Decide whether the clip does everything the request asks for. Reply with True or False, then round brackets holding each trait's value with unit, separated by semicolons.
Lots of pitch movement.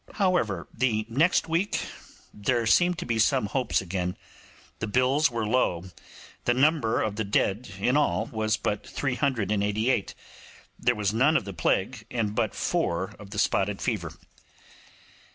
False (4.2 semitones)